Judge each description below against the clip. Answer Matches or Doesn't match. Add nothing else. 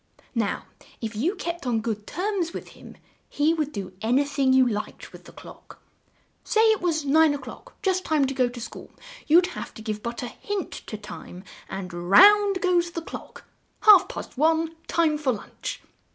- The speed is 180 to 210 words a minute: Matches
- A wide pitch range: Matches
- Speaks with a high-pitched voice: Matches